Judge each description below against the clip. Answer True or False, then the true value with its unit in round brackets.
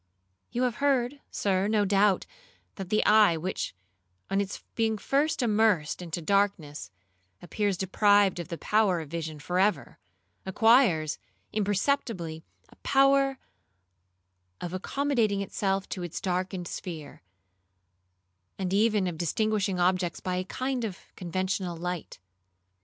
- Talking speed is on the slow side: True (125 wpm)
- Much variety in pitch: False (3.5 semitones)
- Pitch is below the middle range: False (195 Hz)